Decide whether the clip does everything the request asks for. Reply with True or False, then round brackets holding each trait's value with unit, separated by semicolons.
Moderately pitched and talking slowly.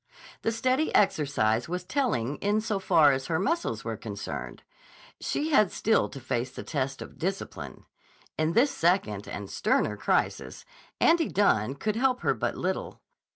False (180 Hz; 155 wpm)